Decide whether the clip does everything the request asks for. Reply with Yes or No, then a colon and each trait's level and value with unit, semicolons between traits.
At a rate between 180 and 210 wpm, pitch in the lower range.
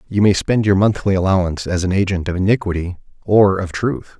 Yes: average, 200 wpm; very low, 95 Hz